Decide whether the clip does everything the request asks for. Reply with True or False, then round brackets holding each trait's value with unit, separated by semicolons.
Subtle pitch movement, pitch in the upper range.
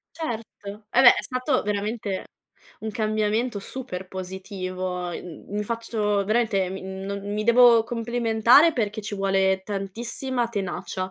False (3.4 semitones; 210 Hz)